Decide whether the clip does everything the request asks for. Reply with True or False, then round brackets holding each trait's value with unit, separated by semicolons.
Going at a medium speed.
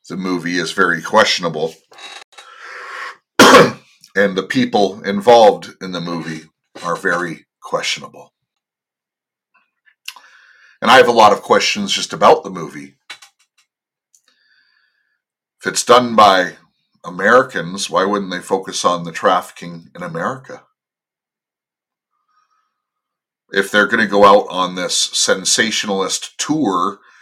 False (110 wpm)